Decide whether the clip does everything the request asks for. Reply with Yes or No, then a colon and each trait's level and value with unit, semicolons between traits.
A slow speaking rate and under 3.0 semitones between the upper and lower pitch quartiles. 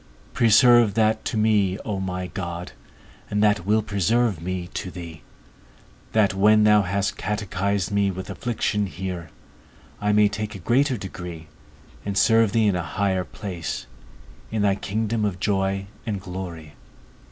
No: average, 150 wpm; narrow, 2.6 semitones